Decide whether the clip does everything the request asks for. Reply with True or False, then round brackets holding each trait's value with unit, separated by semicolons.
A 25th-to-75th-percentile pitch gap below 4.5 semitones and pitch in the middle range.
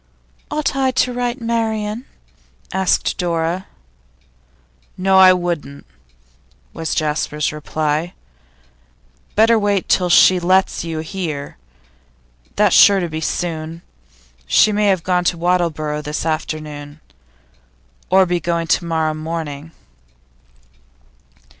True (3.5 semitones; 175 Hz)